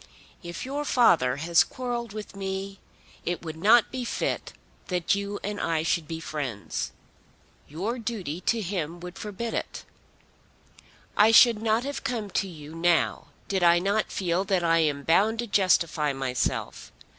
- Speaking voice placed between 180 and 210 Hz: Yes, high, 190 Hz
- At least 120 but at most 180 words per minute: Yes, average, 155 wpm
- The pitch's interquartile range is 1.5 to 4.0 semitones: No, average, 4.8 semitones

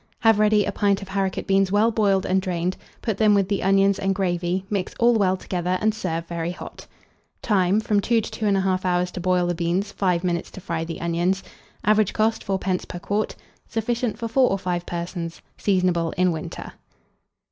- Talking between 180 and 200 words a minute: Yes, average, 195 wpm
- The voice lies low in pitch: No, high, 190 Hz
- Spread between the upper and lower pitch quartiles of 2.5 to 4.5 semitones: Yes, average, 2.8 semitones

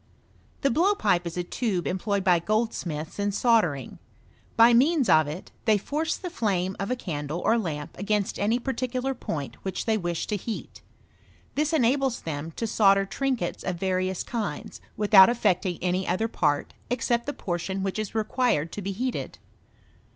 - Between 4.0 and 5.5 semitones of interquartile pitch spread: Yes, average, 5.0 semitones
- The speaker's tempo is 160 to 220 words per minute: Yes, average, 165 wpm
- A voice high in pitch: Yes, high, 205 Hz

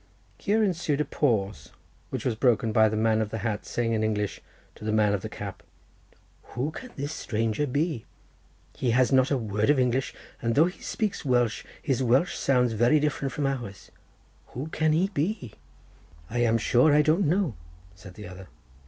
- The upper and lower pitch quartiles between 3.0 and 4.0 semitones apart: No, average, 5.2 semitones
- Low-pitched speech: Yes, low, 125 Hz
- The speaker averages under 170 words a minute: No, average, 190 wpm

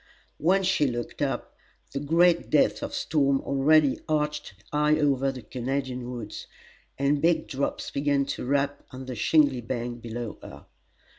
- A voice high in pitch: No, medium, 140 Hz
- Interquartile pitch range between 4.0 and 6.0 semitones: No, average, 2.8 semitones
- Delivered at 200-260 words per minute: No, average, 150 wpm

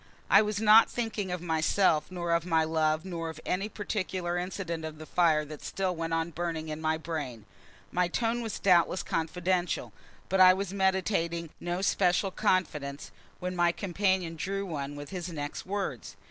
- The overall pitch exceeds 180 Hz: No, medium, 175 Hz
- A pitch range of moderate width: Yes, average, 3.0 semitones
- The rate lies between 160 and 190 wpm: Yes, average, 175 wpm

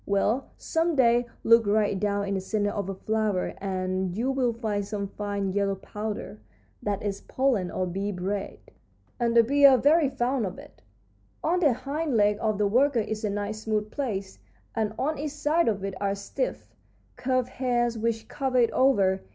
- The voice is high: Yes, high, 215 Hz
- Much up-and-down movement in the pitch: No, average, 4.2 semitones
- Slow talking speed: No, average, 185 wpm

